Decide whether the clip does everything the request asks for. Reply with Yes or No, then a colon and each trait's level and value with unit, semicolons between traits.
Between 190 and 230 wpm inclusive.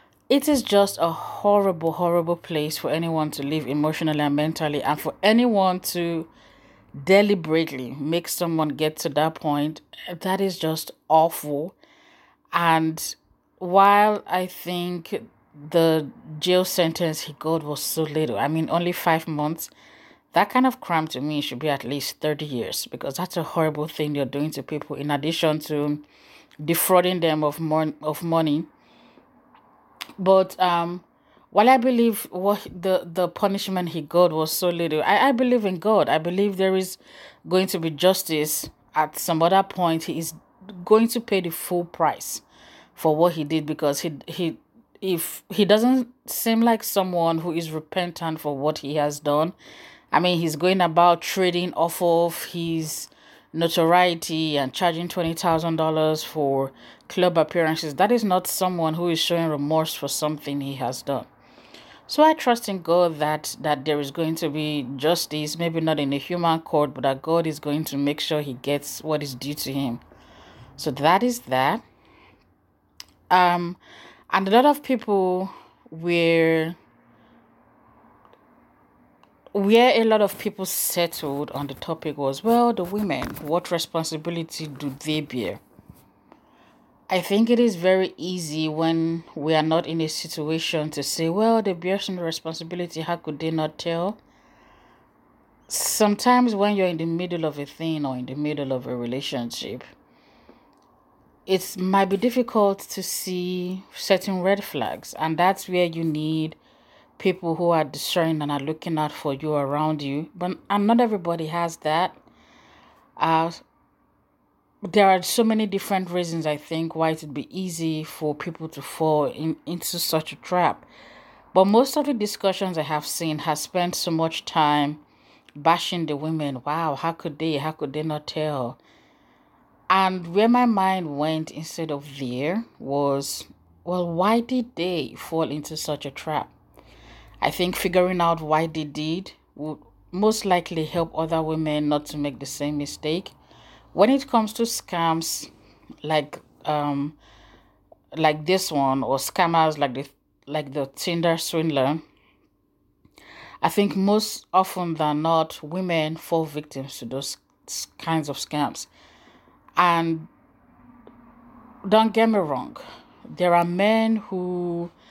No: average, 155 wpm